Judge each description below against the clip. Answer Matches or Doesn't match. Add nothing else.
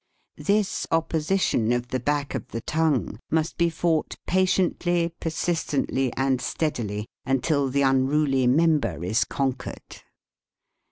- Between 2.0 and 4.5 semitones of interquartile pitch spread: Matches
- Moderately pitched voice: Matches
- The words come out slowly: Matches